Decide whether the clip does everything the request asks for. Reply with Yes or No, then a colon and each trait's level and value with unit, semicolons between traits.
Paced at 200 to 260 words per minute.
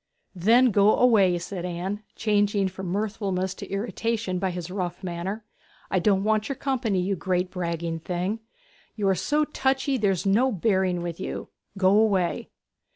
No: average, 155 wpm